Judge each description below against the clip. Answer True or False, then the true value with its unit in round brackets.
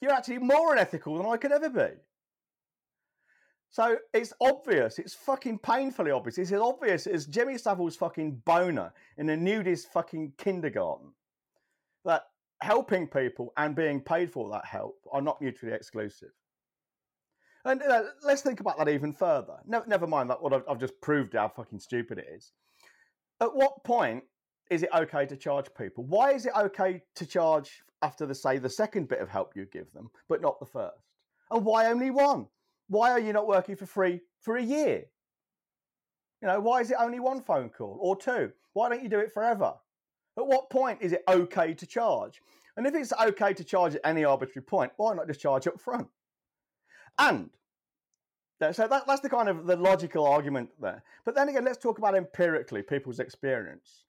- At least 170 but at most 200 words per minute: True (185 wpm)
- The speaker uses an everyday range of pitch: False (8.0 semitones)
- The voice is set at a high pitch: True (195 Hz)